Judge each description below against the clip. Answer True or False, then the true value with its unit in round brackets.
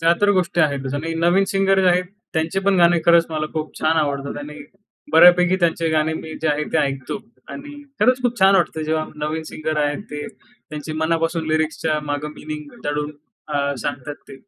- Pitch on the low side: False (160 Hz)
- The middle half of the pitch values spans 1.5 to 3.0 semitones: True (2.7 semitones)